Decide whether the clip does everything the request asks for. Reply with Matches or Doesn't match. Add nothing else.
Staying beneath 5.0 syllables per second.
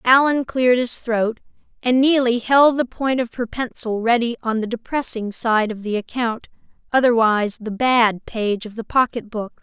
Matches